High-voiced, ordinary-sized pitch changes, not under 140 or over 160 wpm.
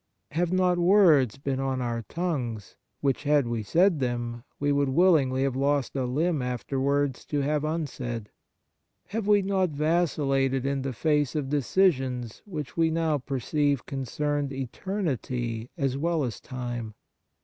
No: medium, 140 Hz; average, 3.9 semitones; average, 145 wpm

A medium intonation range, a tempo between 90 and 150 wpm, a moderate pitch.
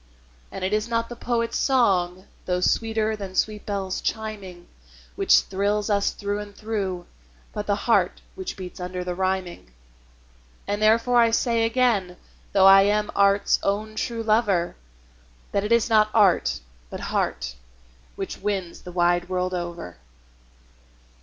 No: average, 3.1 semitones; average, 145 wpm; high, 200 Hz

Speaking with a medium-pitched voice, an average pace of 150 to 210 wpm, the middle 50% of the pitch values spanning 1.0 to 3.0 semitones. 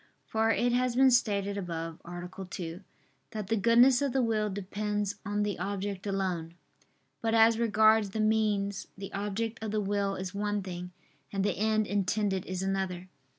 No: high, 205 Hz; average, 170 wpm; narrow, 2.4 semitones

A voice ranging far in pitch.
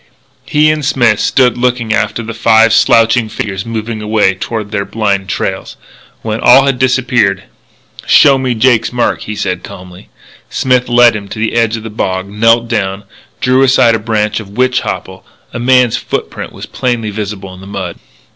No: average, 3.0 semitones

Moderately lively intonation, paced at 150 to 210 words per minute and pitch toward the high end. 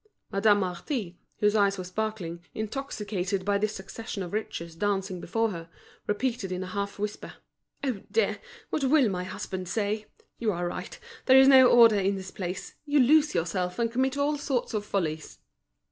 Yes: average, 4.1 semitones; average, 175 wpm; high, 205 Hz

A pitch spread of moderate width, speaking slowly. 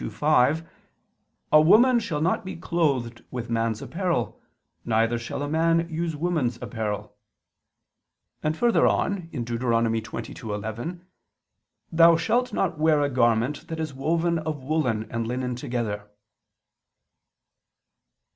No: wide, 6.0 semitones; slow, 120 wpm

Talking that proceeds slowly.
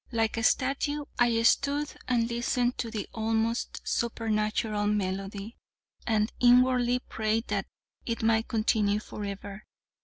Yes: slow, 120 wpm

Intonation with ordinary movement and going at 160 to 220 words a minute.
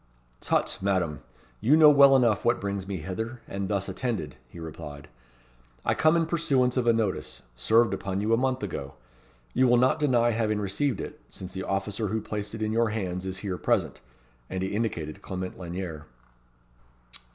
Yes: average, 4.1 semitones; average, 180 wpm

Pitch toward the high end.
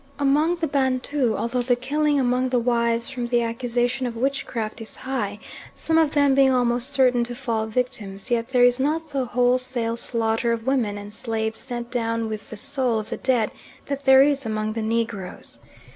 Yes: high, 245 Hz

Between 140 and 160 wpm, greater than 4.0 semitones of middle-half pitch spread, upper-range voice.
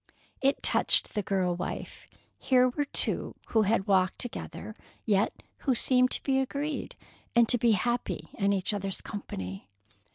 Yes: average, 155 wpm; average, 4.6 semitones; high, 220 Hz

